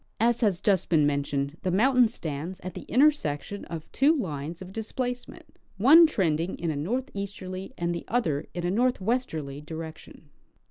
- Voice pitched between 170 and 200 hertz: Yes, medium, 185 Hz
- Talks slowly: No, average, 155 wpm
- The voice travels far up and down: Yes, wide, 7.1 semitones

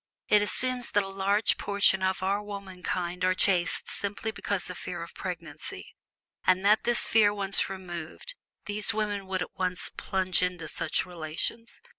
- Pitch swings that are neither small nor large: No, narrow, 2.2 semitones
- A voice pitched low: No, high, 190 Hz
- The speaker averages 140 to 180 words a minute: Yes, average, 160 wpm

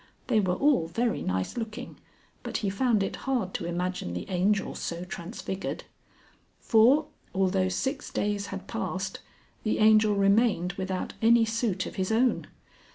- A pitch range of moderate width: Yes, average, 3.6 semitones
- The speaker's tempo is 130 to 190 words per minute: Yes, average, 150 wpm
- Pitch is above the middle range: Yes, high, 200 Hz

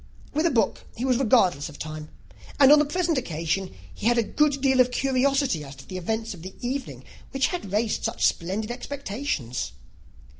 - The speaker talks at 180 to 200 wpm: Yes, average, 190 wpm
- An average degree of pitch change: No, wide, 6.8 semitones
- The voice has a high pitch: Yes, high, 235 Hz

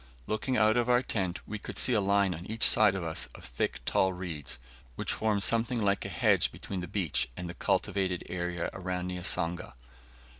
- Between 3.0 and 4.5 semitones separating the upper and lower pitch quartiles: Yes, average, 3.5 semitones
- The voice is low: Yes, very low, 95 Hz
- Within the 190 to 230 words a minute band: Yes, average, 195 wpm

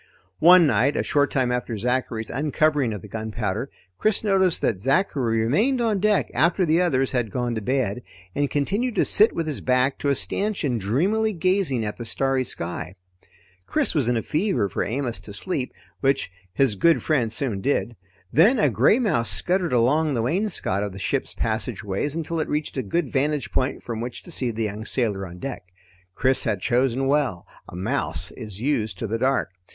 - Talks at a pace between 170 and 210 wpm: Yes, average, 190 wpm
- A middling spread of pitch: No, wide, 5.9 semitones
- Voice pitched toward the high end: No, low, 130 Hz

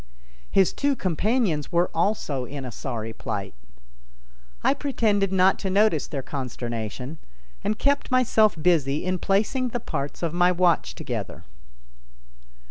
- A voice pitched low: No, medium, 180 Hz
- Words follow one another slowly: Yes, slow, 130 wpm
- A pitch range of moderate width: No, wide, 7.6 semitones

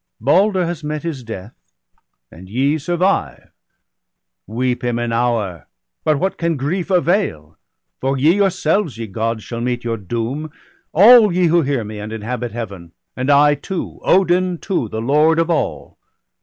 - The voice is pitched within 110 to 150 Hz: Yes, medium, 140 Hz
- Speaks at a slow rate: No, average, 160 wpm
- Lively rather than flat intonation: Yes, wide, 7.0 semitones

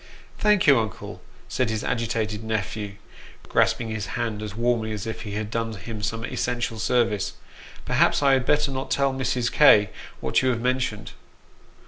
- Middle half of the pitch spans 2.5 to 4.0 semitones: Yes, average, 2.8 semitones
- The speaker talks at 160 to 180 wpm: Yes, average, 175 wpm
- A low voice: Yes, low, 115 Hz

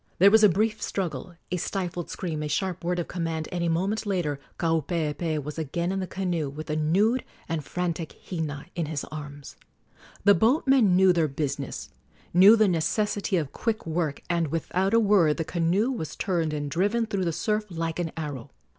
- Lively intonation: No, average, 3.7 semitones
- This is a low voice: No, medium, 170 Hz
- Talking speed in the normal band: Yes, average, 190 wpm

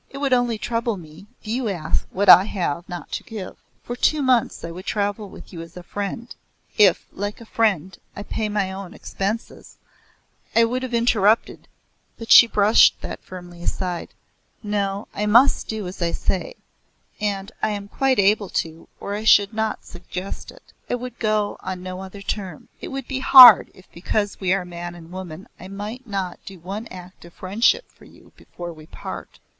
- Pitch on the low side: No, high, 200 Hz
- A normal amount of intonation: Yes, average, 3.5 semitones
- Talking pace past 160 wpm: Yes, average, 195 wpm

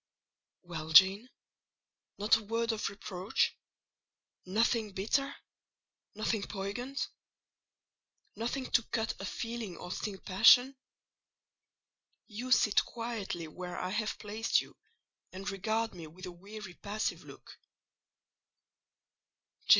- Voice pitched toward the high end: Yes, high, 210 Hz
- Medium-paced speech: No, slow, 105 wpm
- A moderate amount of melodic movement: Yes, average, 3.3 semitones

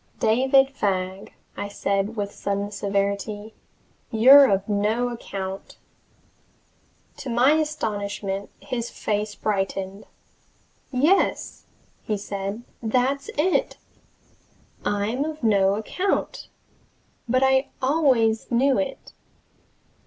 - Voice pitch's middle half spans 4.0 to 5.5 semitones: Yes, average, 4.8 semitones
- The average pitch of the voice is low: No, high, 220 Hz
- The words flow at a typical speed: No, slow, 95 wpm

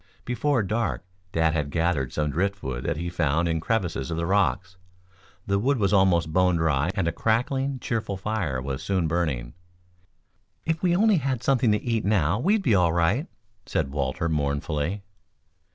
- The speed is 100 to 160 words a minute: No, average, 170 wpm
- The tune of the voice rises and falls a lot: Yes, wide, 5.9 semitones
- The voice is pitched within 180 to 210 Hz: No, very low, 90 Hz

